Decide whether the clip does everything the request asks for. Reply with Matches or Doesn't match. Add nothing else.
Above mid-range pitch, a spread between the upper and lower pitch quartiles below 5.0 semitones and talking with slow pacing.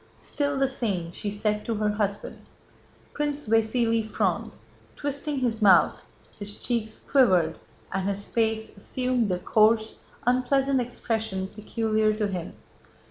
Matches